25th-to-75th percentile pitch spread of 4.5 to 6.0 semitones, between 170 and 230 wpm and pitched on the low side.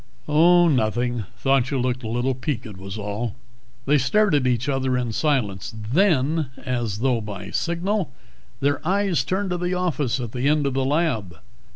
Yes: average, 5.1 semitones; average, 175 wpm; low, 130 Hz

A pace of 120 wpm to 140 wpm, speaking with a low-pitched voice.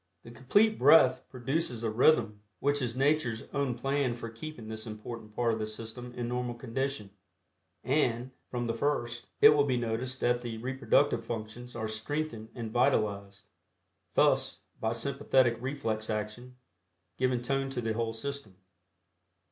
No: average, 150 wpm; low, 120 Hz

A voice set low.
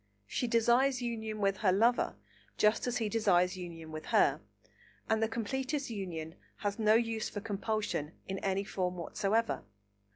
No: high, 215 Hz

